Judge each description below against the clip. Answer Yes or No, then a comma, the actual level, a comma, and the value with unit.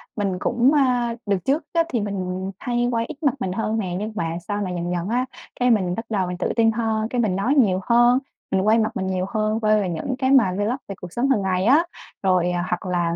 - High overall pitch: Yes, high, 215 Hz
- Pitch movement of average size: Yes, average, 4.4 semitones